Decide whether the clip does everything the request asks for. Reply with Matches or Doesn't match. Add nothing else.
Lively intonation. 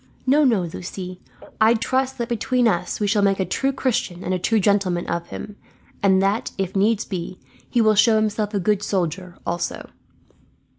Doesn't match